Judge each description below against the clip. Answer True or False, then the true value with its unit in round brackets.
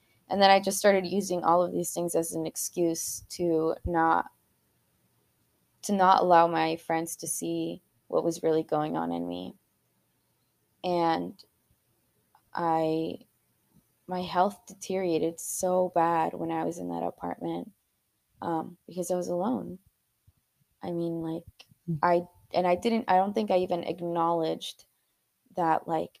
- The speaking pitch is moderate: True (170 Hz)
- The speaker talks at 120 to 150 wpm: True (140 wpm)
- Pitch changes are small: True (2.2 semitones)